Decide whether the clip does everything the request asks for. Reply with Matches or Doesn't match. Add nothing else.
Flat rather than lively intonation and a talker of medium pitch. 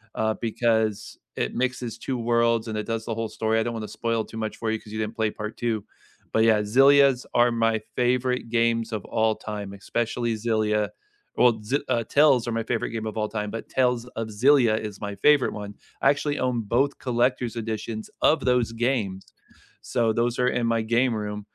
Doesn't match